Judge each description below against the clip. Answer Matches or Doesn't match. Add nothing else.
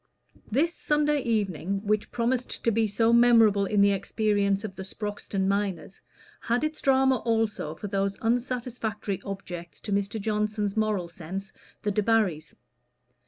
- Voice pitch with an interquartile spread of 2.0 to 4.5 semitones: Matches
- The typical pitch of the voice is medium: Doesn't match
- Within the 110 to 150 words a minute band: Matches